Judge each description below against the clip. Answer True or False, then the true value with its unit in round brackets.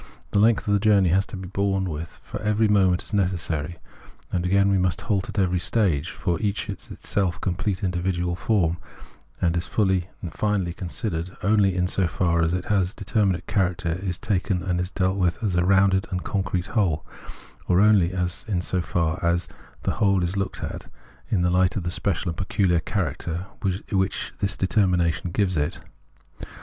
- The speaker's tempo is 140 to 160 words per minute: False (180 wpm)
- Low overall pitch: True (95 Hz)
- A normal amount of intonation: False (2.1 semitones)